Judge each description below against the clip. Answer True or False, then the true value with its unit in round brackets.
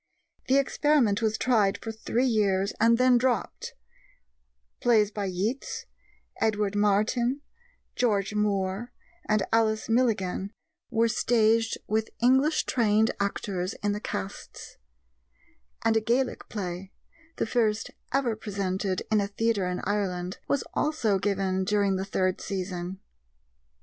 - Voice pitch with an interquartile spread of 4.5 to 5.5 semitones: False (3.0 semitones)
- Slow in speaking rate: True (125 wpm)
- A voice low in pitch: False (210 Hz)